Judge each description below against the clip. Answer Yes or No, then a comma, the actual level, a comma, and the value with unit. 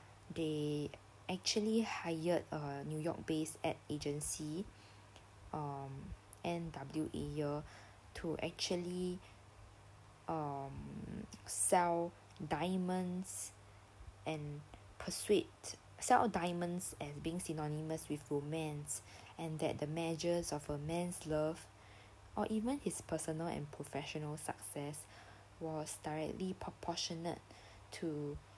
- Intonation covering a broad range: Yes, wide, 8.2 semitones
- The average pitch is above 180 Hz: No, medium, 150 Hz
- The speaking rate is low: Yes, slow, 90 wpm